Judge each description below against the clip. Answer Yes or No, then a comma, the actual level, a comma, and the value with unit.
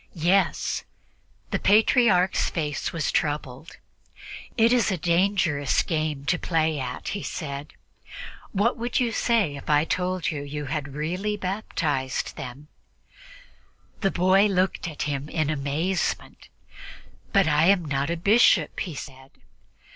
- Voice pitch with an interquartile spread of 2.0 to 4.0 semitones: No, average, 4.7 semitones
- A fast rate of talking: No, slow, 135 wpm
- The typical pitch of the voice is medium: Yes, medium, 165 Hz